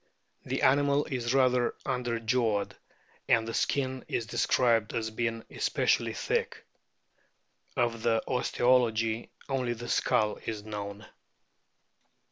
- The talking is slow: Yes, slow, 105 wpm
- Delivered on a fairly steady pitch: Yes, narrow, 2.2 semitones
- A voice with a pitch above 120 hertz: No, low, 115 Hz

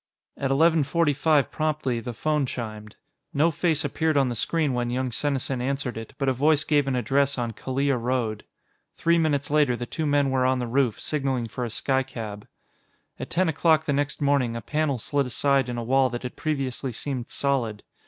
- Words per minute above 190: Yes, average, 200 wpm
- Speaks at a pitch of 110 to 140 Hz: Yes, low, 135 Hz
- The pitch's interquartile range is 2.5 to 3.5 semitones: Yes, average, 3.0 semitones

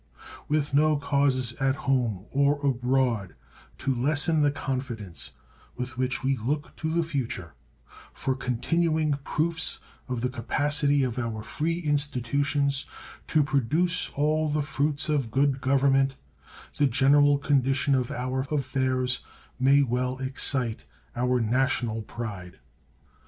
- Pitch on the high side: No, low, 135 Hz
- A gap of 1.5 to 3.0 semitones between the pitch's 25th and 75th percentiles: Yes, narrow, 2.5 semitones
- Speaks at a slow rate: Yes, slow, 125 wpm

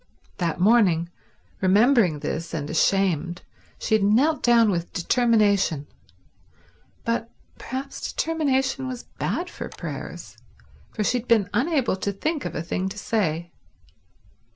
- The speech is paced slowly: Yes, slow, 130 wpm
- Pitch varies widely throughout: Yes, wide, 6.0 semitones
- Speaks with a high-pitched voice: Yes, high, 210 Hz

